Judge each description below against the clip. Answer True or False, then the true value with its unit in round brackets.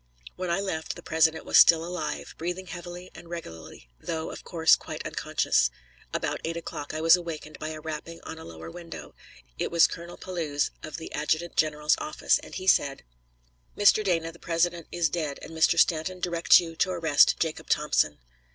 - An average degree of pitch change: False (1.9 semitones)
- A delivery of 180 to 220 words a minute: True (185 wpm)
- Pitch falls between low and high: True (165 Hz)